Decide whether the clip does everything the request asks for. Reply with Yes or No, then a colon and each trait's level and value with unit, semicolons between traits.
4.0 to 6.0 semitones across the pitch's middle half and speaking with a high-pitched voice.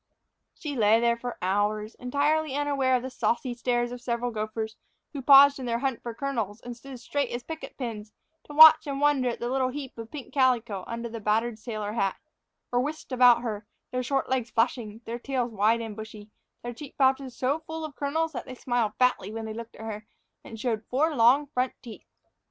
No: average, 3.2 semitones; high, 245 Hz